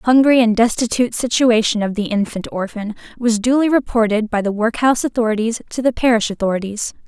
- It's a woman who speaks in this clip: Yes, female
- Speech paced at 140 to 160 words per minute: No, average, 170 wpm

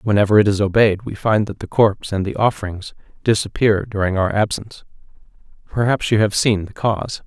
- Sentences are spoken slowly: No, average, 180 wpm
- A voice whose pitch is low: Yes, low, 105 Hz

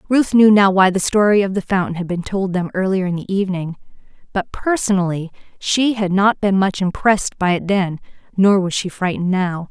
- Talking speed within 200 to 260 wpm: Yes, fast, 205 wpm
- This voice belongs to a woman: Yes, female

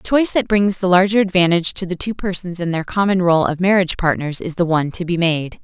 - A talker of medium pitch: Yes, medium, 180 Hz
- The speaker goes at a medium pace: No, fast, 255 wpm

